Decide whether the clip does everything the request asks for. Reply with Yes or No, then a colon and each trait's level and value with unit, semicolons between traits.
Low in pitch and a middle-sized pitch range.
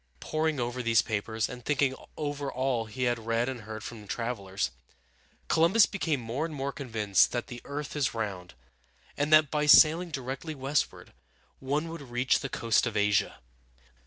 Yes: low, 125 Hz; average, 4.5 semitones